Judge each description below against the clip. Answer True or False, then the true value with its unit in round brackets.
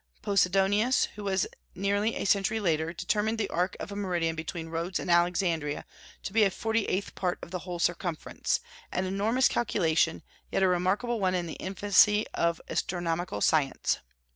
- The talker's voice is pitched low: False (185 Hz)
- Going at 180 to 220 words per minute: False (165 wpm)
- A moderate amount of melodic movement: True (3.0 semitones)